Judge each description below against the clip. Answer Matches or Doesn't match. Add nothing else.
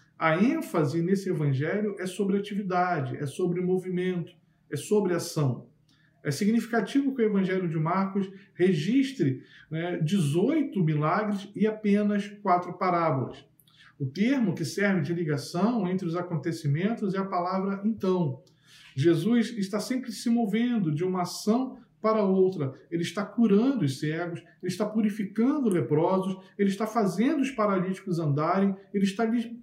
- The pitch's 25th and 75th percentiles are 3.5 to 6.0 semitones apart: Matches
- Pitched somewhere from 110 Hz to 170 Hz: Doesn't match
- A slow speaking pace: Doesn't match